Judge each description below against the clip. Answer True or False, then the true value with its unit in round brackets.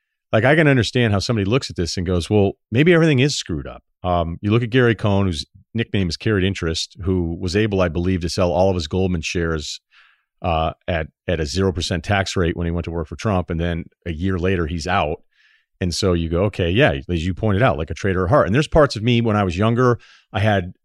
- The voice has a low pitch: True (95 Hz)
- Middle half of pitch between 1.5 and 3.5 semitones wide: False (4.0 semitones)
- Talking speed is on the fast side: True (255 wpm)